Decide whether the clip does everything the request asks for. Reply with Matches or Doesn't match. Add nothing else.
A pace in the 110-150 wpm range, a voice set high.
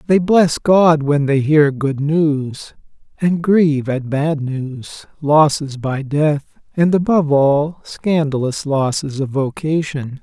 Doesn't match